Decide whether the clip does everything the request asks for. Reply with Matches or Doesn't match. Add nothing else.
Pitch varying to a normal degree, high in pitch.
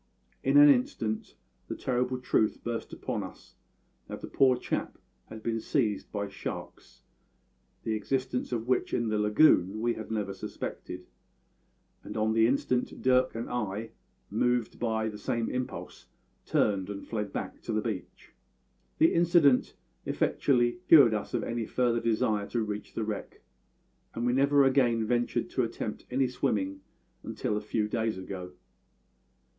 Doesn't match